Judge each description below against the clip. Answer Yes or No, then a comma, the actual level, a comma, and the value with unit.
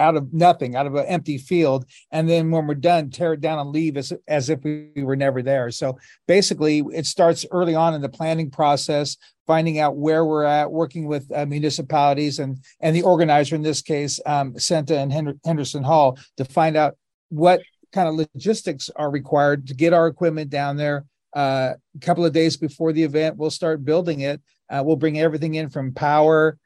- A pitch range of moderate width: No, narrow, 2.1 semitones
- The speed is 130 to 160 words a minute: No, fast, 205 wpm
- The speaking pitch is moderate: Yes, medium, 155 Hz